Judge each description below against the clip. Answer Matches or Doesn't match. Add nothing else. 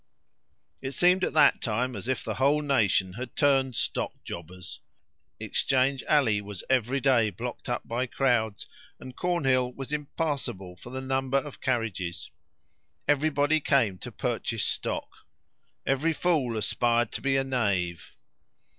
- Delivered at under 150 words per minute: Matches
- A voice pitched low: Matches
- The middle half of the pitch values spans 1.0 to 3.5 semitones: Doesn't match